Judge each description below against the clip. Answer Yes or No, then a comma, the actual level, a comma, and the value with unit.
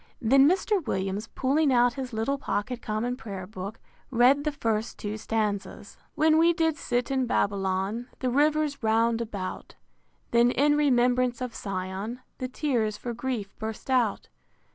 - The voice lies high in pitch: Yes, high, 240 Hz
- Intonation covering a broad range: No, average, 4.1 semitones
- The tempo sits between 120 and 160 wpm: Yes, average, 155 wpm